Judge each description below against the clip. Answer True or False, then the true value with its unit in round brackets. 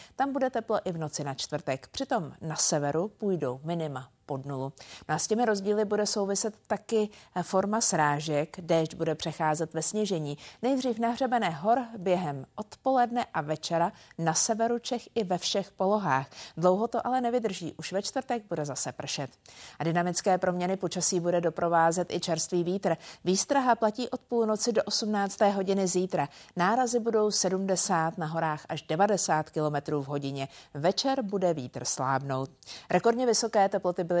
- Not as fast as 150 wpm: False (155 wpm)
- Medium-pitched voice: True (180 Hz)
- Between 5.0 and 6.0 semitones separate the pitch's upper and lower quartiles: True (5.5 semitones)